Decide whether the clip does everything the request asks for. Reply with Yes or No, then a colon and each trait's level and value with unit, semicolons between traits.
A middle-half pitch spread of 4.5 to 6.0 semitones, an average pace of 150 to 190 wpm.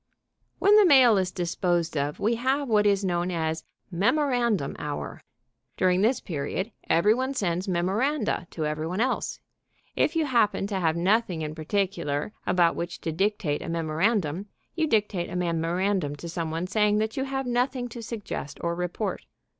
Yes: wide, 5.5 semitones; average, 170 wpm